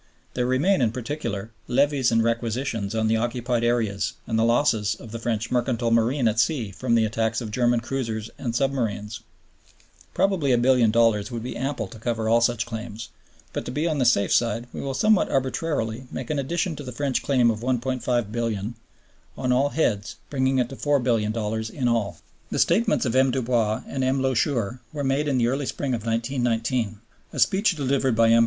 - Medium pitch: No, low, 120 Hz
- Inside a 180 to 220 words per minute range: Yes, average, 190 wpm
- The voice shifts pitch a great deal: No, average, 2.9 semitones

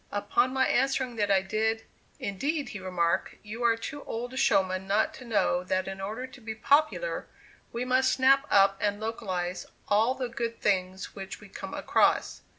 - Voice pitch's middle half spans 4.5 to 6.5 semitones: Yes, average, 5.0 semitones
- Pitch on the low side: No, high, 220 Hz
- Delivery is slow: No, average, 180 wpm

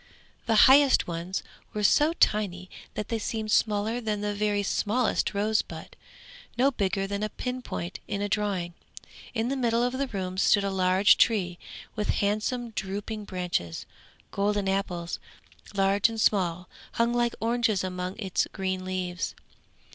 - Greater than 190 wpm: No, average, 145 wpm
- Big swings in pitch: No, average, 3.2 semitones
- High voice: Yes, high, 205 Hz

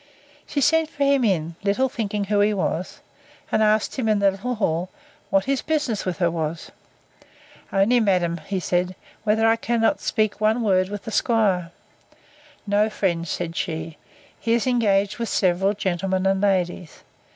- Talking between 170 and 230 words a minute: No, average, 160 wpm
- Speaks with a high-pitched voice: Yes, high, 200 Hz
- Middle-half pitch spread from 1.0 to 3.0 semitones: No, average, 3.7 semitones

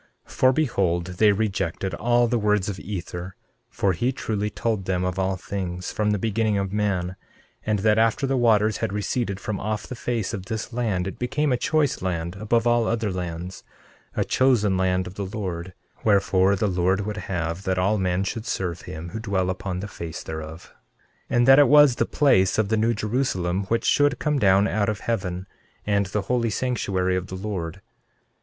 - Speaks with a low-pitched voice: Yes, low, 100 Hz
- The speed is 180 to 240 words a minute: Yes, average, 200 wpm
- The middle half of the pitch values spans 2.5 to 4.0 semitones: Yes, average, 3.5 semitones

